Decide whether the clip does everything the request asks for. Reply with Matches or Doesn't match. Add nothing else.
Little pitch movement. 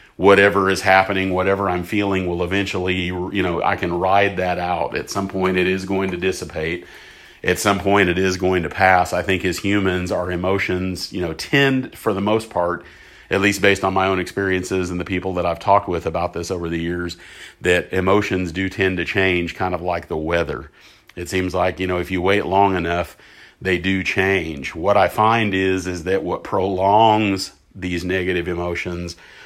Matches